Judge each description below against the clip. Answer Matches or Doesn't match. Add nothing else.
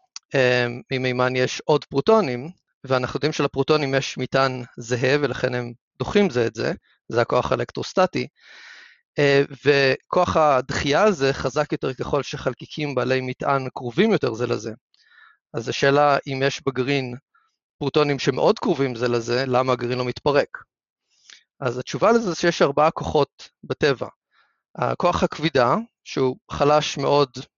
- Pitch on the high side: Doesn't match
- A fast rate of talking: Doesn't match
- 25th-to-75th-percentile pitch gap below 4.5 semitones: Matches